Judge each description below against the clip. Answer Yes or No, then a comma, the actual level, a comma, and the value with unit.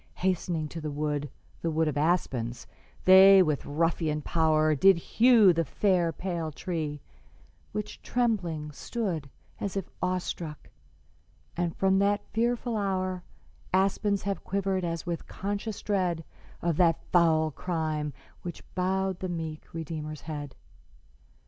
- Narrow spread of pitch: No, average, 3.6 semitones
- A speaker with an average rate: No, slow, 130 wpm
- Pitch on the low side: No, medium, 170 Hz